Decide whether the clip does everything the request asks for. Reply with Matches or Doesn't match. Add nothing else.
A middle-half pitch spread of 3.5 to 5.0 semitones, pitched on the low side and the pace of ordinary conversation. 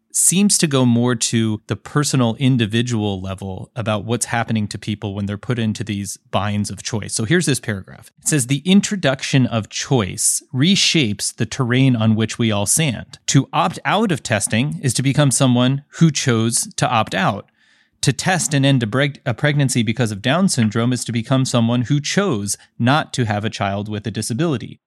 Matches